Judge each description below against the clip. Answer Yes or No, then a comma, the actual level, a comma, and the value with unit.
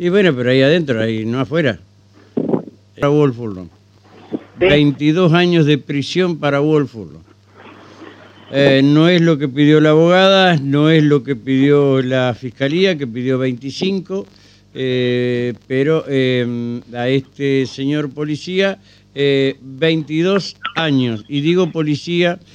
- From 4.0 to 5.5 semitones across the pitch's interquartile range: Yes, average, 4.5 semitones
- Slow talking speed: Yes, slow, 120 wpm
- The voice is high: No, medium, 140 Hz